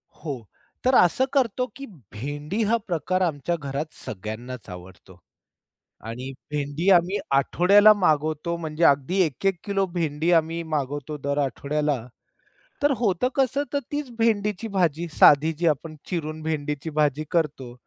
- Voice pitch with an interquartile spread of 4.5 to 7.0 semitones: Yes, average, 4.8 semitones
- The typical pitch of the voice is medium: Yes, medium, 155 Hz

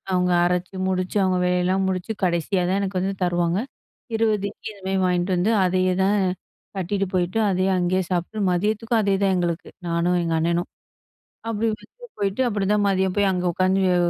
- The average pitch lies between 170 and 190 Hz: Yes, medium, 185 Hz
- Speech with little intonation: Yes, narrow, 1.8 semitones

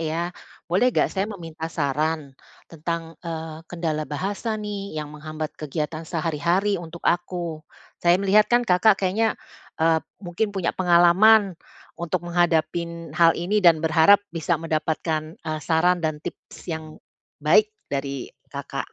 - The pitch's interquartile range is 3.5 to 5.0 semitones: No, average, 2.7 semitones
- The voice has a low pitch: No, medium, 170 Hz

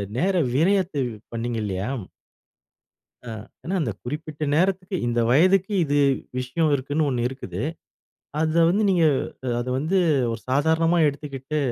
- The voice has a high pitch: No, medium, 150 Hz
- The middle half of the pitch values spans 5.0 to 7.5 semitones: Yes, average, 5.3 semitones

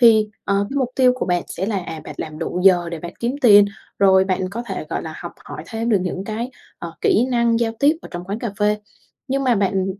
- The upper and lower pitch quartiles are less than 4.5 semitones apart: Yes, average, 4.1 semitones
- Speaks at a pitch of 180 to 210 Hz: Yes, high, 205 Hz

